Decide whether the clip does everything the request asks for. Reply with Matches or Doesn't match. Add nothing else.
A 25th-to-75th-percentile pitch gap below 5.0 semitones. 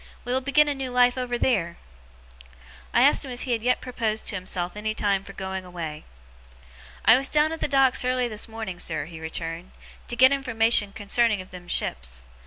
Doesn't match